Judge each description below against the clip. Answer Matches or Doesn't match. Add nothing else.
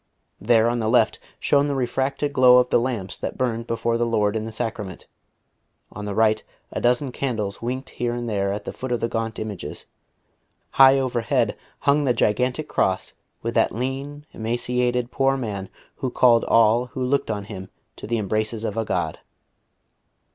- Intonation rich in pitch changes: Doesn't match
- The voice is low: Matches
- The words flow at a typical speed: Matches